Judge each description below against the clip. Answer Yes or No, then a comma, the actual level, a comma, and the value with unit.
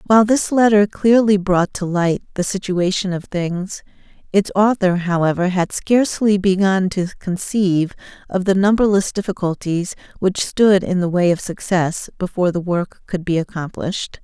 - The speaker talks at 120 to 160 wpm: Yes, average, 150 wpm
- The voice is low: No, high, 190 Hz